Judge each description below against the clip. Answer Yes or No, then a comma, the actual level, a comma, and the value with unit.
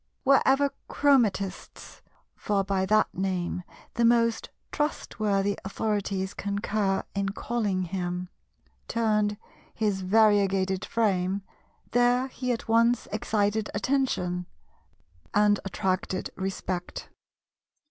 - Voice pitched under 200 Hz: No, high, 205 Hz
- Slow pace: Yes, slow, 85 wpm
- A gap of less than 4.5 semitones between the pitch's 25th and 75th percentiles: Yes, average, 3.0 semitones